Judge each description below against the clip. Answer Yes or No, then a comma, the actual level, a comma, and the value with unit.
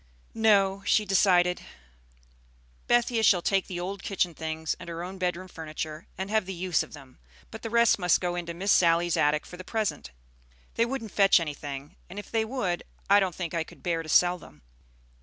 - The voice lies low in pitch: No, medium, 180 Hz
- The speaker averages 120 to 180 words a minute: No, average, 195 wpm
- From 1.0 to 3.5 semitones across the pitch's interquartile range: Yes, average, 3.1 semitones